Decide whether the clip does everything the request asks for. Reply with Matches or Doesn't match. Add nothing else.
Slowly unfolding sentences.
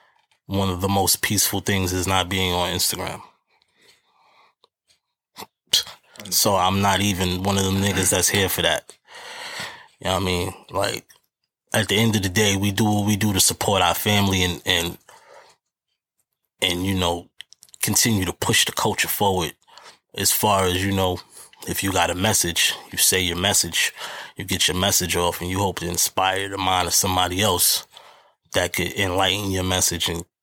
Doesn't match